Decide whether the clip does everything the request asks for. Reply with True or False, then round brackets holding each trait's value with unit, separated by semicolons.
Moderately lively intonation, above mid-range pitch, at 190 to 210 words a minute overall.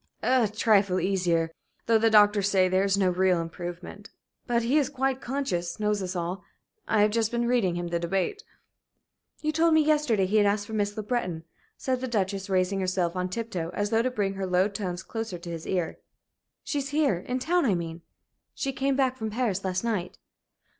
True (4.7 semitones; 205 Hz; 200 wpm)